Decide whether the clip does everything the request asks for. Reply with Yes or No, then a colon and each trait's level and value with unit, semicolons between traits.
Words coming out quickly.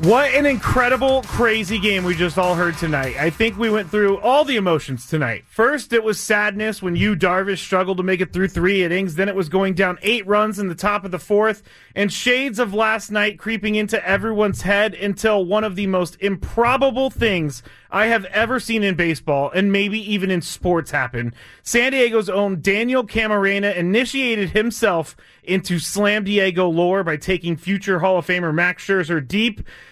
No: average, 190 wpm